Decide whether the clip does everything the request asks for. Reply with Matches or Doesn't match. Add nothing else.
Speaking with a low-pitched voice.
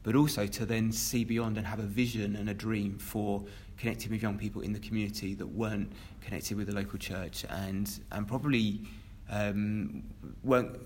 Matches